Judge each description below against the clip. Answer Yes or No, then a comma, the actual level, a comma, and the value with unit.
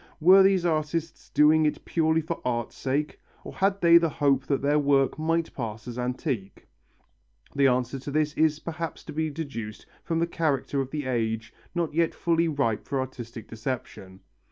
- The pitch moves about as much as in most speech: Yes, average, 4.4 semitones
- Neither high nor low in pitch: Yes, medium, 145 Hz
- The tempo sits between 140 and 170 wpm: No, average, 180 wpm